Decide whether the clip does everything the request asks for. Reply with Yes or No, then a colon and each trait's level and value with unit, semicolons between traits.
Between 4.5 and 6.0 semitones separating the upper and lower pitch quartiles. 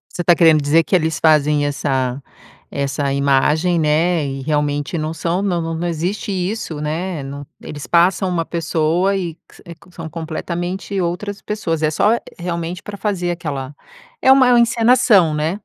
No: average, 3.2 semitones